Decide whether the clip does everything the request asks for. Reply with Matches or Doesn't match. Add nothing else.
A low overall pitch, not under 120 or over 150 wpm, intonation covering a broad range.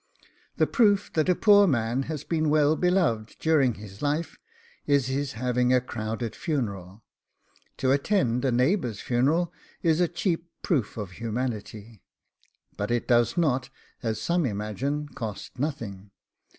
Matches